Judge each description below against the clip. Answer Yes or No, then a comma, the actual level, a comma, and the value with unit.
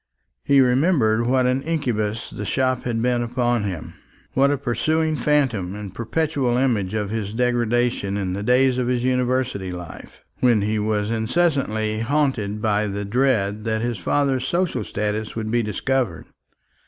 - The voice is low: Yes, low, 120 Hz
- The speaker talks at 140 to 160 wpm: Yes, average, 155 wpm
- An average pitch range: Yes, average, 3.7 semitones